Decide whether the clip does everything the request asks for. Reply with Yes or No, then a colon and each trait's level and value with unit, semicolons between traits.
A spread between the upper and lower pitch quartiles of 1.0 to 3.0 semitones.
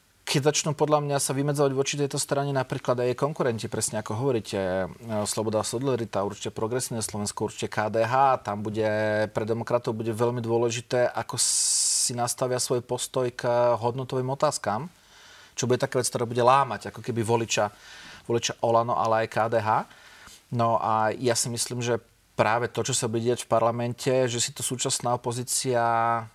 Yes: narrow, 2.4 semitones